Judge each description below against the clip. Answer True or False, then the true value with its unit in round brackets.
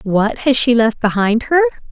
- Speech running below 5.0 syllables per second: True (4.5 syllables/s)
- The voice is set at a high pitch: True (245 Hz)